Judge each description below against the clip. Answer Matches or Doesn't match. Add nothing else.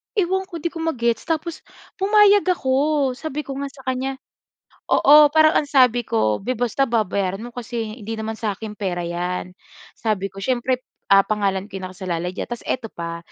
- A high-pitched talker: Matches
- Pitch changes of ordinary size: Doesn't match